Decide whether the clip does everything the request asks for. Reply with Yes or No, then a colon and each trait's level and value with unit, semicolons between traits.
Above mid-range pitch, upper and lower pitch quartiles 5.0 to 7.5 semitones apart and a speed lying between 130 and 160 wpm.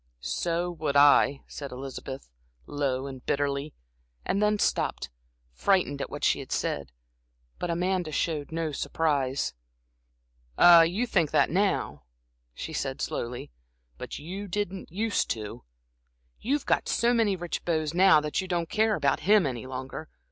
No: medium, 160 Hz; average, 5.3 semitones; average, 150 wpm